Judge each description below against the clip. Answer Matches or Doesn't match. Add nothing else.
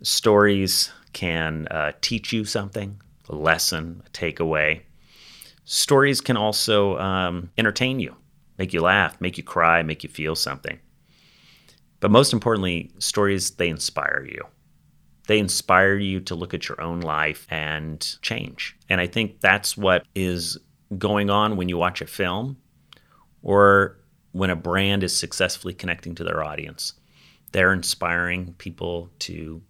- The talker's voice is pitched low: Matches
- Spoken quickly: Doesn't match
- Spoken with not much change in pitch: Doesn't match